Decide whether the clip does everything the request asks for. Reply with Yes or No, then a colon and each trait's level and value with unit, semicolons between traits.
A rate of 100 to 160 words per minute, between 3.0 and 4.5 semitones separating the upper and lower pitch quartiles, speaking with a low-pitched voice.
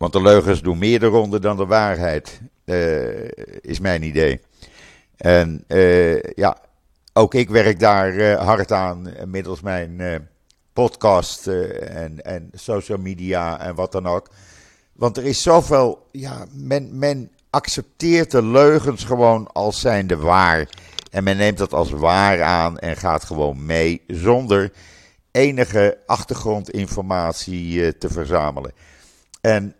Yes: average, 140 wpm; average, 4.2 semitones; very low, 95 Hz